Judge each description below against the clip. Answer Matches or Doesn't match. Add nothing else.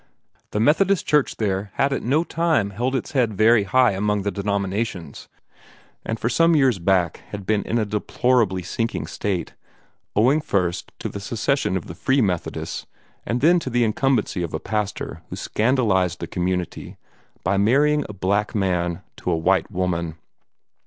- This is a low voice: Matches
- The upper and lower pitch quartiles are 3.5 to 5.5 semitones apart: Matches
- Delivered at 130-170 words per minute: Matches